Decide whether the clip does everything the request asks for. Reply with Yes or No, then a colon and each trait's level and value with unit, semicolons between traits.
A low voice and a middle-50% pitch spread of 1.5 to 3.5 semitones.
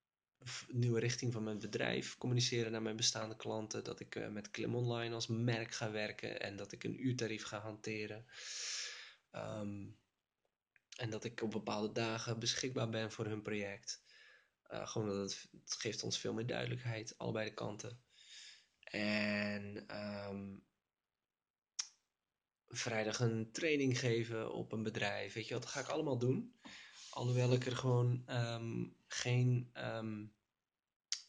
Yes: low, 115 Hz; narrow, 2.4 semitones